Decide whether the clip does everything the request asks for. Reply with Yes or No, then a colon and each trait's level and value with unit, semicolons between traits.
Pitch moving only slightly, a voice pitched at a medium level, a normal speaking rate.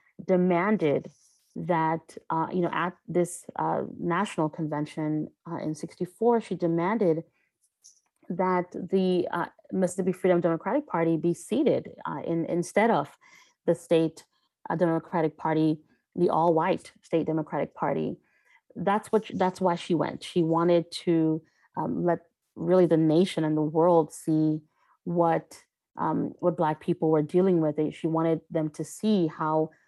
Yes: narrow, 2.1 semitones; medium, 170 Hz; average, 145 wpm